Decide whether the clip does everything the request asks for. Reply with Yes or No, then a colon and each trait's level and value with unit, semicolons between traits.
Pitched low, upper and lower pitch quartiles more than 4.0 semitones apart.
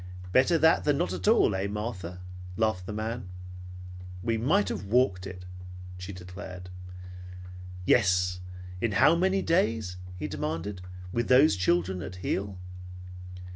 Yes: low, 100 Hz; average, 5.2 semitones